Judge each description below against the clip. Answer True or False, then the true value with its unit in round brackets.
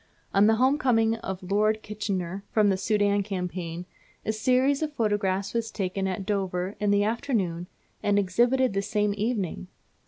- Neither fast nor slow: True (160 wpm)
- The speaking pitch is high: True (205 Hz)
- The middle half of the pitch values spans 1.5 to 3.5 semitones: True (2.8 semitones)